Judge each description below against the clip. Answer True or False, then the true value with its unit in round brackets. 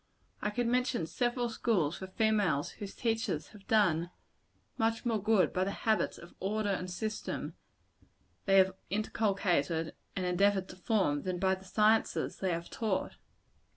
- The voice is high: True (195 Hz)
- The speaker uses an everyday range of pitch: True (3.2 semitones)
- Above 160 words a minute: False (155 wpm)